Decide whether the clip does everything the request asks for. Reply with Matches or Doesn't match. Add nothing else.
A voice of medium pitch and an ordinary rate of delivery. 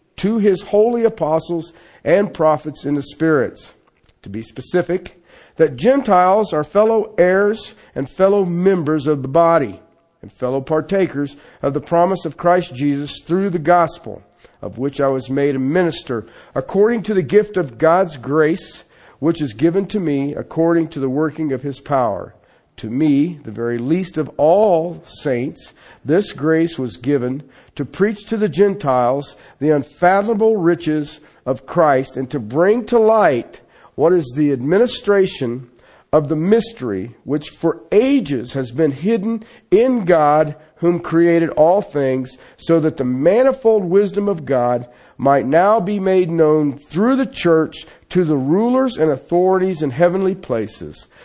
Matches